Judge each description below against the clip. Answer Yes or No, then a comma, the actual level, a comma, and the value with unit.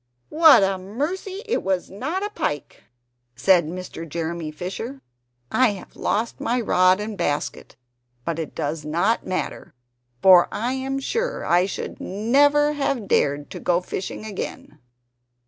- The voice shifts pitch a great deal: Yes, wide, 7.8 semitones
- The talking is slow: No, average, 145 wpm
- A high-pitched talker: Yes, high, 195 Hz